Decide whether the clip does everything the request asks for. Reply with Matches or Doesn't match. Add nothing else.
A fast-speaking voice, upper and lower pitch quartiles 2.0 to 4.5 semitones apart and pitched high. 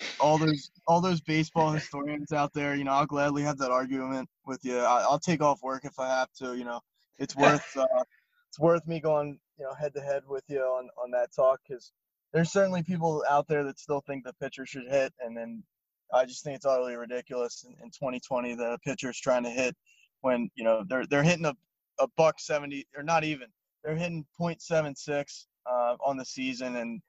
Doesn't match